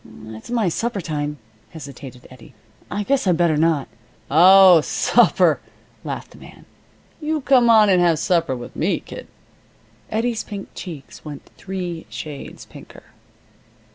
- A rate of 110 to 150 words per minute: Yes, average, 140 wpm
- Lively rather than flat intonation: Yes, wide, 5.8 semitones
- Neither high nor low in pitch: Yes, medium, 175 Hz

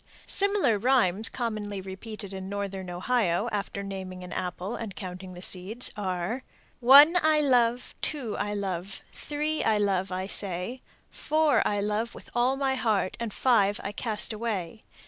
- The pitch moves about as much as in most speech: Yes, average, 4.3 semitones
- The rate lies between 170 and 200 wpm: No, average, 155 wpm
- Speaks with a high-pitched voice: Yes, high, 210 Hz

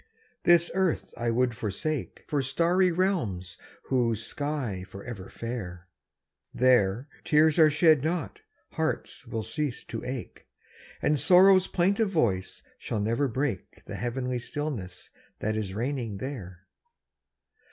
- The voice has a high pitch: No, low, 125 Hz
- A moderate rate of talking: No, slow, 120 wpm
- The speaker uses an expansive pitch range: Yes, wide, 6.3 semitones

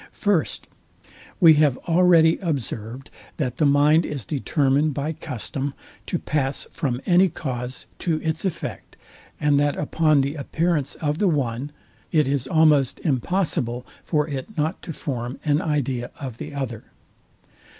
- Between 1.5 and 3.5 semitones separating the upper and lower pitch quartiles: Yes, average, 3.2 semitones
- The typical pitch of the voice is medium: Yes, medium, 145 Hz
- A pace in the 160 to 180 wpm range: No, average, 140 wpm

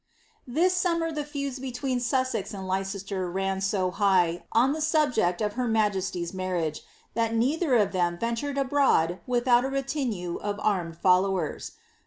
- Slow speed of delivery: No, average, 150 wpm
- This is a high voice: Yes, high, 220 Hz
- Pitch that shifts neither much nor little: No, wide, 6.1 semitones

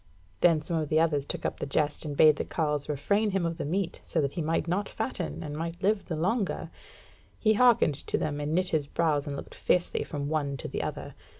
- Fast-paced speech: Yes, fast, 235 wpm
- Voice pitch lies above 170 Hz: No, medium, 155 Hz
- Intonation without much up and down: No, average, 3.4 semitones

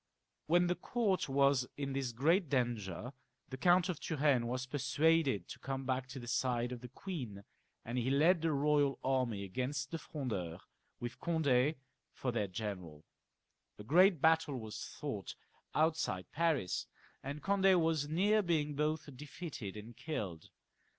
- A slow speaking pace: No, average, 150 wpm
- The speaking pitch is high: No, low, 135 Hz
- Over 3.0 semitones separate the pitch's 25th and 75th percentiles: Yes, average, 5.0 semitones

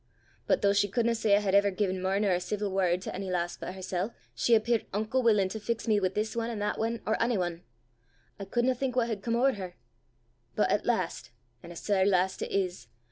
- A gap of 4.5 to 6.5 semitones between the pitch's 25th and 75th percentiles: No, average, 3.4 semitones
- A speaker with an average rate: No, fast, 240 wpm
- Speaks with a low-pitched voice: No, high, 205 Hz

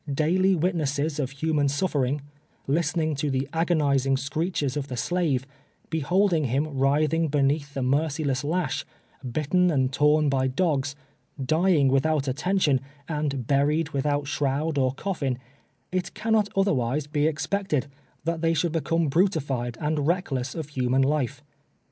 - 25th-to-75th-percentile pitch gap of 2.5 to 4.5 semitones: Yes, average, 3.1 semitones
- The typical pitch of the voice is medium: Yes, medium, 150 Hz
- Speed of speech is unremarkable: Yes, average, 150 wpm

